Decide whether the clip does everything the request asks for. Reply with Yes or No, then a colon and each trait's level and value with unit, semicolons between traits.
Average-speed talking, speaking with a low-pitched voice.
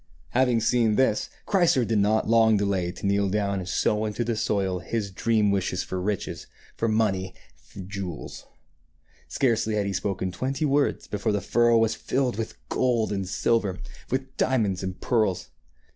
Yes: average, 165 wpm; low, 105 Hz